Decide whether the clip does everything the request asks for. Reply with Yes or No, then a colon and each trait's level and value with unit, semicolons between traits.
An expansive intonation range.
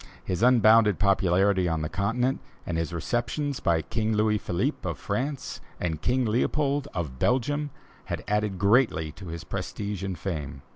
Yes: wide, 5.8 semitones